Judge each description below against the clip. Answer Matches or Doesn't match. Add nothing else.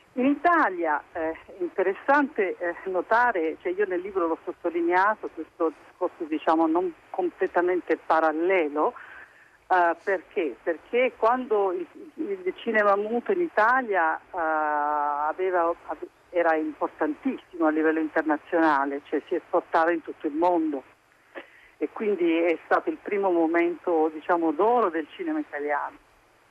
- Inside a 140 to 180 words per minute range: Doesn't match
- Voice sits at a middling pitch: Matches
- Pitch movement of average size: Doesn't match